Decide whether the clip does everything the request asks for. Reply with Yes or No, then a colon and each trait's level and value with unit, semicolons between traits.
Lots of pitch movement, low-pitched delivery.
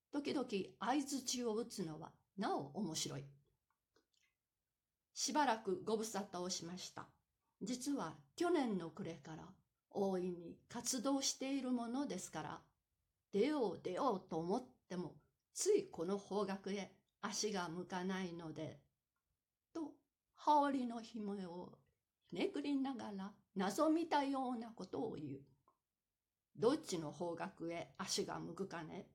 No: wide, 6.8 semitones; high, 200 Hz